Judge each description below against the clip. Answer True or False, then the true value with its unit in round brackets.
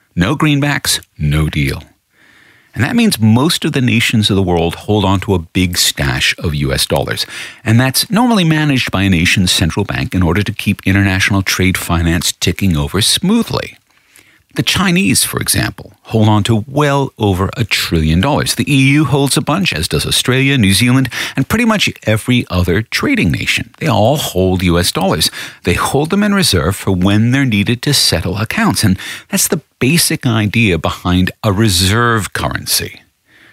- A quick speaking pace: False (175 wpm)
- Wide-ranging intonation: True (6.6 semitones)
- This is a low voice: True (110 Hz)